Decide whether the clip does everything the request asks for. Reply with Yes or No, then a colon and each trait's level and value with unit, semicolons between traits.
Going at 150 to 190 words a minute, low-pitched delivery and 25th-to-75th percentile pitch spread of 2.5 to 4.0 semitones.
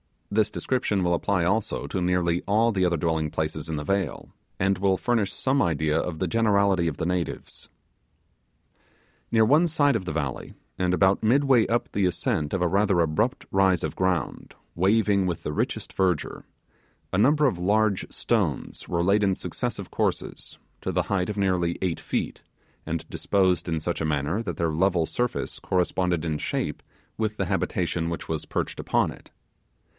Yes: average, 175 wpm; very low, 95 Hz; average, 3.6 semitones